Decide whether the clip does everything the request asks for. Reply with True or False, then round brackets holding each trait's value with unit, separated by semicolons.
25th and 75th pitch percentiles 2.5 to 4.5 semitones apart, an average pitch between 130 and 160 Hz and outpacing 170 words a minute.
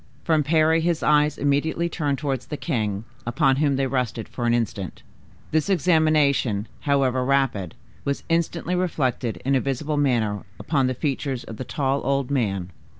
False (3.8 semitones; 140 Hz; 160 wpm)